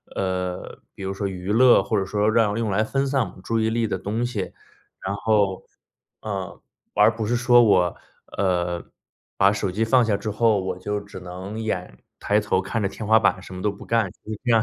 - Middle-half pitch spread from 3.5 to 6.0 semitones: No, average, 2.8 semitones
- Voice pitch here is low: Yes, low, 105 Hz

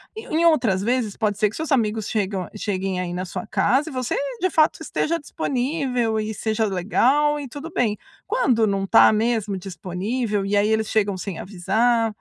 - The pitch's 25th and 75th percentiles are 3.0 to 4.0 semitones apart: No, average, 4.5 semitones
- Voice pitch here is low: No, high, 220 Hz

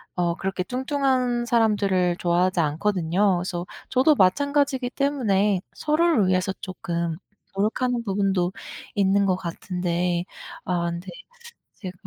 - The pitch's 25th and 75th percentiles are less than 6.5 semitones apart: Yes, average, 5.3 semitones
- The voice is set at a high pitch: Yes, high, 195 Hz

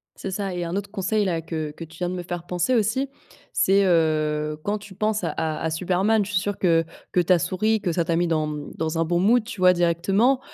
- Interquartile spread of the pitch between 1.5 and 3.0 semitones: No, average, 3.6 semitones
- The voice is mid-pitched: Yes, medium, 180 Hz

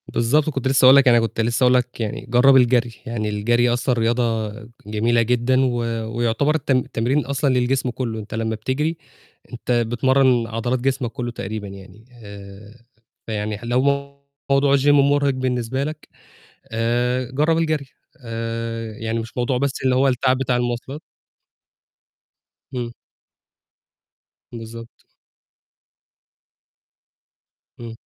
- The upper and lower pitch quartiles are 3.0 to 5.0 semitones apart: No, narrow, 2.5 semitones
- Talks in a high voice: No, low, 120 Hz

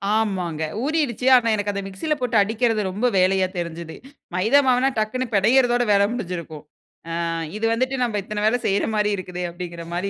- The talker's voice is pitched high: Yes, high, 210 Hz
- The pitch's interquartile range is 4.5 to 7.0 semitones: Yes, average, 4.9 semitones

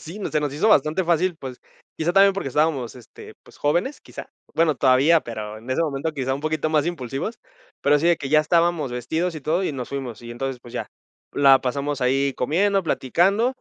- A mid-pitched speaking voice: Yes, medium, 150 Hz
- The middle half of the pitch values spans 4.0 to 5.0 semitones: Yes, average, 4.3 semitones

